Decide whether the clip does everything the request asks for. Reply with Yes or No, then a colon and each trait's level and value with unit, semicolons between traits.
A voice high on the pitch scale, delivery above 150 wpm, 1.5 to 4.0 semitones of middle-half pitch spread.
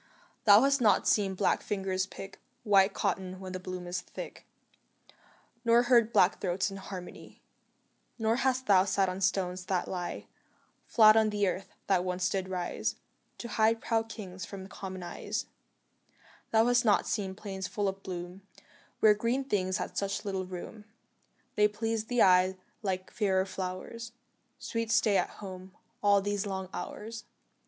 Yes: high, 195 Hz; average, 160 wpm; average, 2.8 semitones